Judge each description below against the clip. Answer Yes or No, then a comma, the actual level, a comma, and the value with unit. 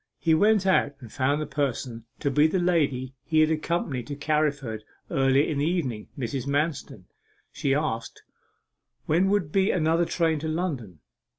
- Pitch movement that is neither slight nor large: Yes, average, 3.6 semitones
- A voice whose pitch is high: No, medium, 150 Hz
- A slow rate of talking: No, average, 165 wpm